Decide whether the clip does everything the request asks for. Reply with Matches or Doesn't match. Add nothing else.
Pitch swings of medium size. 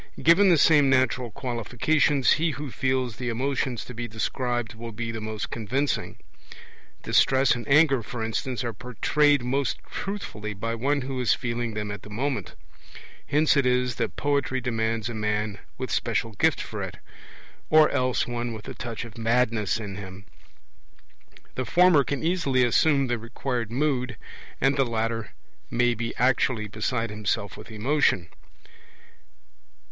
Matches